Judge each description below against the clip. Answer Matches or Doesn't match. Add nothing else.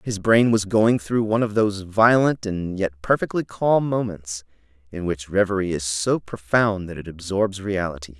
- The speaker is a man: Matches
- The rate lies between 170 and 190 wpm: Matches